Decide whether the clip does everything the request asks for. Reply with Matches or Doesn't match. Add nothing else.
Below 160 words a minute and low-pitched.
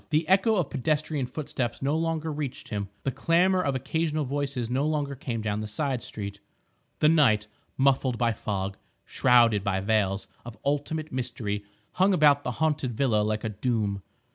Doesn't match